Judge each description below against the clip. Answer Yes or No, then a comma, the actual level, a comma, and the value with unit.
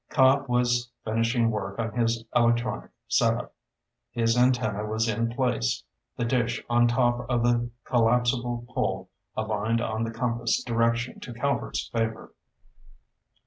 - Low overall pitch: Yes, low, 120 Hz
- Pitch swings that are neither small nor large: No, narrow, 1.2 semitones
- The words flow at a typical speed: No, slow, 130 wpm